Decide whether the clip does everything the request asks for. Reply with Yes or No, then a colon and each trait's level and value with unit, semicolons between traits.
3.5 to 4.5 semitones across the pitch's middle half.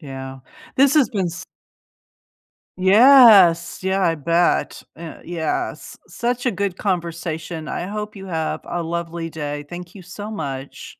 Yes: average, 3.8 semitones